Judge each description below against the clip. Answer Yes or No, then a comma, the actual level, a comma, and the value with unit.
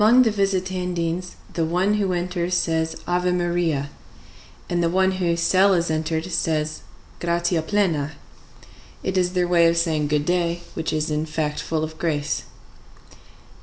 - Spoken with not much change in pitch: Yes, narrow, 2.3 semitones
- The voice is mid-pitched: Yes, medium, 170 Hz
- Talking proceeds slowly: No, average, 155 wpm